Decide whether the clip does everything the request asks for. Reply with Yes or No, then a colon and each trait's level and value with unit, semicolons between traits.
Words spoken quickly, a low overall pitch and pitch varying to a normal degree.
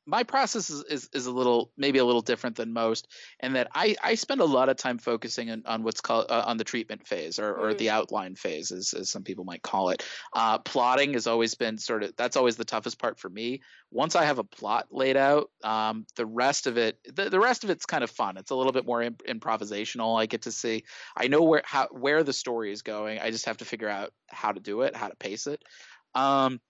Yes: fast, 255 wpm; low, 120 Hz; average, 3.2 semitones